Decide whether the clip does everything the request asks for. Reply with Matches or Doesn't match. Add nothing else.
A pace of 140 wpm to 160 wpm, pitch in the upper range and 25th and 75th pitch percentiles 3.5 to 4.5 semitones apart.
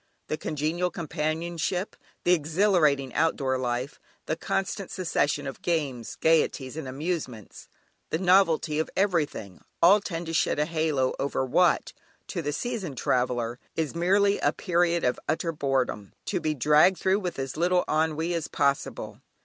Doesn't match